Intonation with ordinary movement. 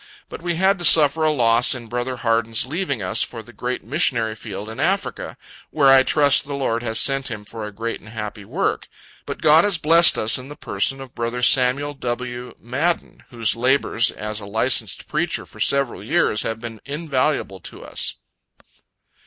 Yes: average, 4.2 semitones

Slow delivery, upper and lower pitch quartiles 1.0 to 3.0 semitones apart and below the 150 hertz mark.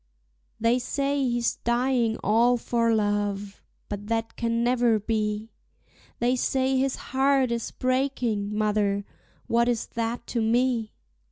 No: slow, 125 wpm; average, 2.7 semitones; high, 235 Hz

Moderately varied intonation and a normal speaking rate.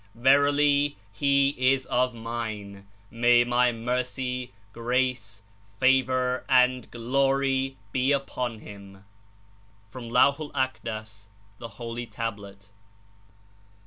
No: average, 3.7 semitones; slow, 95 wpm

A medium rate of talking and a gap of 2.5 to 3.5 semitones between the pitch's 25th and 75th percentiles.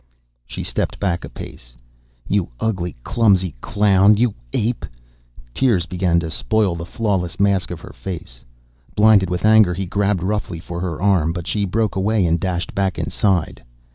Yes: average, 165 wpm; average, 3.0 semitones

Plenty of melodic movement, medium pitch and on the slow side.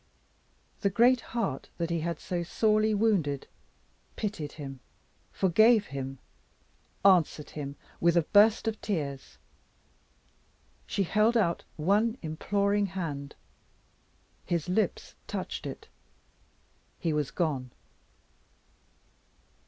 Yes: wide, 5.9 semitones; medium, 175 Hz; slow, 100 wpm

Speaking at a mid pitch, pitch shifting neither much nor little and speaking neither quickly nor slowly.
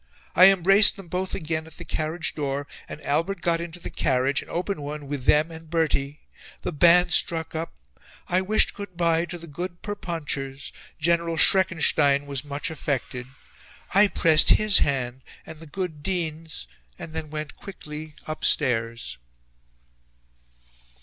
Yes: medium, 160 Hz; average, 3.2 semitones; average, 150 wpm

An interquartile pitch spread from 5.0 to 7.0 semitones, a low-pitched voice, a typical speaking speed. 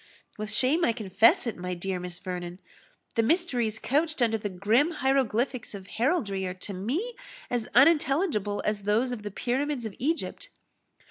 No: wide, 5.4 semitones; high, 230 Hz; average, 160 wpm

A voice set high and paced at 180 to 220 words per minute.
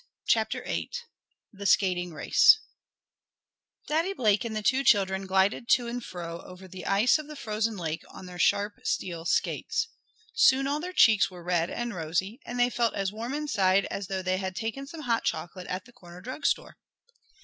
Yes: high, 205 Hz; average, 185 wpm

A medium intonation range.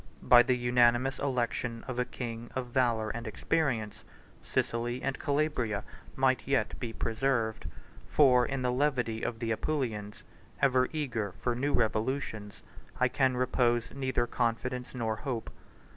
No: narrow, 2.3 semitones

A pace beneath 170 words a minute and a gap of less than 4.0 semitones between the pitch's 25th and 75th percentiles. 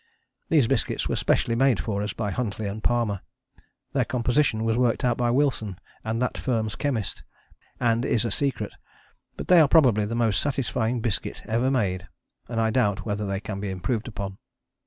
No: average, 180 wpm; average, 3.3 semitones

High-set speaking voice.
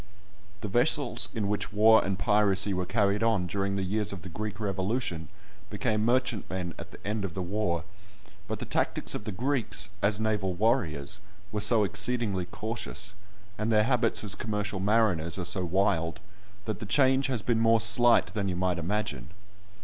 No: low, 105 Hz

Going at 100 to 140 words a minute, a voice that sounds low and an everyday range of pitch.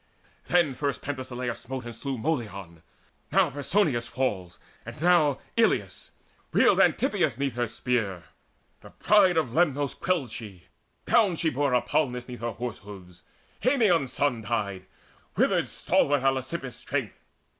Yes: slow, 135 wpm; low, 130 Hz; average, 4.1 semitones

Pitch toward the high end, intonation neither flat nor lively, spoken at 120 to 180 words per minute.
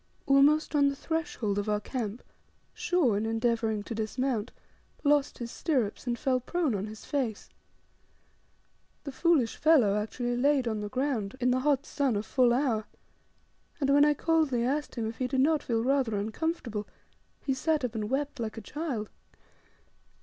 Yes: very high, 255 Hz; average, 4.4 semitones; average, 170 wpm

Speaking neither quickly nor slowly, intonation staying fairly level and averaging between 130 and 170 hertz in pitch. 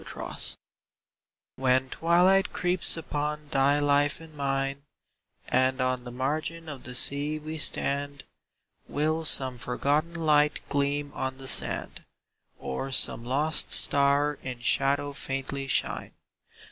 No: slow, 120 wpm; narrow, 2.3 semitones; medium, 140 Hz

